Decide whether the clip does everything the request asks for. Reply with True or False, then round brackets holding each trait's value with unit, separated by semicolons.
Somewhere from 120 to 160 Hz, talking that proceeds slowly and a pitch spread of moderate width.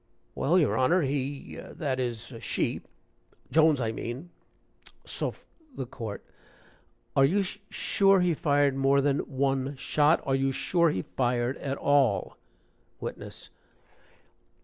True (140 Hz; 125 wpm; 3.4 semitones)